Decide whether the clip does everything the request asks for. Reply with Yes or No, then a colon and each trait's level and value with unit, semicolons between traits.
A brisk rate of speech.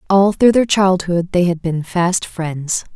No: average, 185 wpm